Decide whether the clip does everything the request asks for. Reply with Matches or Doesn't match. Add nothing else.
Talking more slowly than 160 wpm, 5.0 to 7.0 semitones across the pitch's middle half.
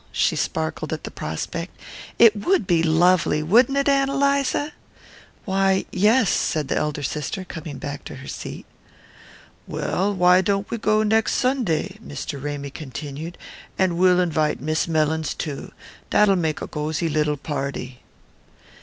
Matches